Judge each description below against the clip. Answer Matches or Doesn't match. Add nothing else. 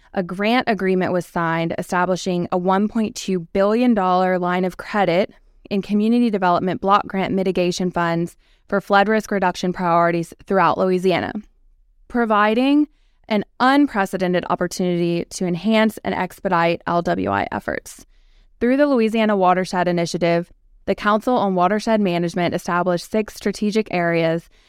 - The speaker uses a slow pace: Matches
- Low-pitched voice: Doesn't match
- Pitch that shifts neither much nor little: Matches